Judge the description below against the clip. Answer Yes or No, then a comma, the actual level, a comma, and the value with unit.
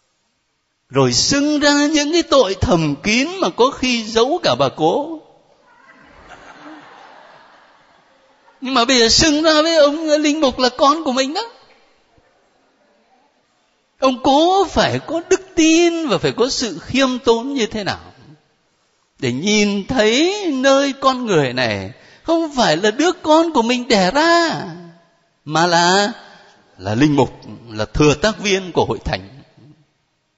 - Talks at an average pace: No, slow, 145 wpm